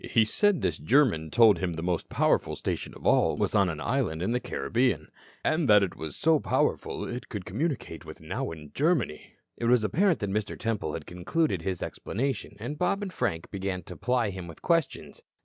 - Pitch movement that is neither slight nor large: No, wide, 8.1 semitones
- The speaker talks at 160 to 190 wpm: No, average, 200 wpm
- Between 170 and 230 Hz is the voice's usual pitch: No, low, 110 Hz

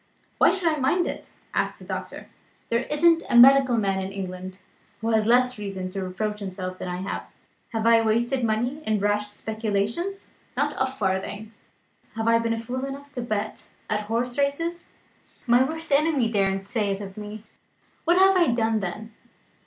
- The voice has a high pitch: Yes, high, 225 Hz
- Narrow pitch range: No, average, 4.5 semitones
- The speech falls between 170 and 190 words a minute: Yes, average, 175 wpm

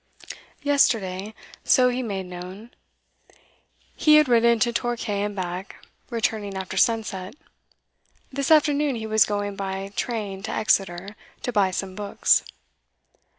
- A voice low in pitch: No, high, 210 Hz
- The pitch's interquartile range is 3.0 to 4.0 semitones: Yes, average, 3.7 semitones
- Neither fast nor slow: No, slow, 125 wpm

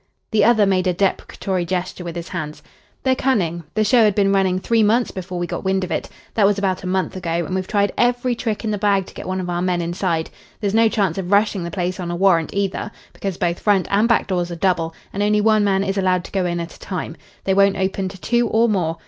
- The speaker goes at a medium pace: No, fast, 260 wpm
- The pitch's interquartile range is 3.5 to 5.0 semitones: No, narrow, 2.6 semitones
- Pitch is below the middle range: No, high, 190 Hz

